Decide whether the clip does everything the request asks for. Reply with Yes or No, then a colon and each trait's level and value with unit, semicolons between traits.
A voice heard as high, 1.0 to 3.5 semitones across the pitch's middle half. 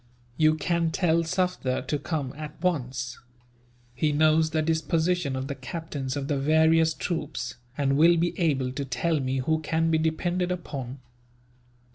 No: medium, 155 Hz; average, 3.1 semitones